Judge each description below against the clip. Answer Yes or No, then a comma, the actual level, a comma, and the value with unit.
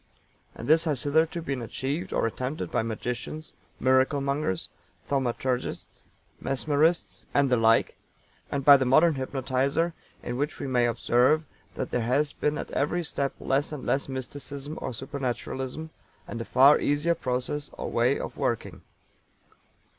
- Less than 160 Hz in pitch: Yes, low, 135 Hz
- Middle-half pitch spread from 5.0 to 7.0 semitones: No, average, 2.7 semitones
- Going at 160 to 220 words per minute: No, average, 145 wpm